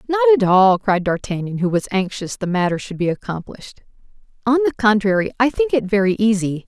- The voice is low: No, high, 205 Hz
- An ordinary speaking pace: Yes, average, 190 wpm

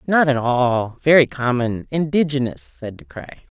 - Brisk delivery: No, average, 150 wpm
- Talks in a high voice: No, low, 135 Hz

